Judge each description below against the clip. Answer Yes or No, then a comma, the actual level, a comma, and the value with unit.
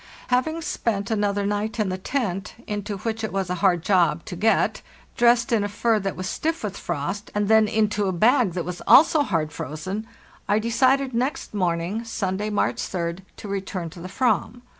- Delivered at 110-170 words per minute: No, average, 185 wpm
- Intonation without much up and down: No, average, 3.6 semitones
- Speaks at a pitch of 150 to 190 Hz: No, high, 205 Hz